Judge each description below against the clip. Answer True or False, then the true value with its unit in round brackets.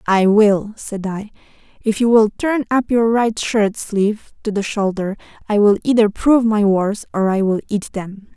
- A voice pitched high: True (210 Hz)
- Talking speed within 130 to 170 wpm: False (195 wpm)